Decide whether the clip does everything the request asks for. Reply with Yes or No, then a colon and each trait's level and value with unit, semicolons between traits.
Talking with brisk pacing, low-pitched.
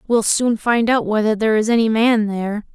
No: fast, 220 wpm; high, 220 Hz